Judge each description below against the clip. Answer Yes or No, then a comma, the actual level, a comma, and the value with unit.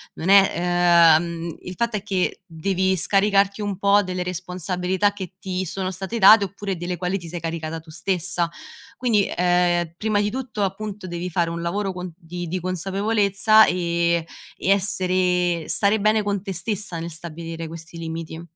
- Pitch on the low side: No, medium, 180 Hz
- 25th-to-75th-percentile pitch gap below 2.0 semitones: No, narrow, 2.6 semitones